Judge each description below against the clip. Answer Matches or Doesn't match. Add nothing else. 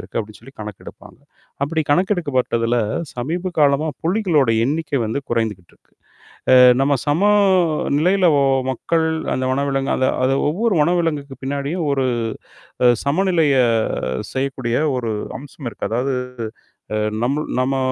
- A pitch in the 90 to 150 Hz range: Matches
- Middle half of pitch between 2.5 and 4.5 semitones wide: Matches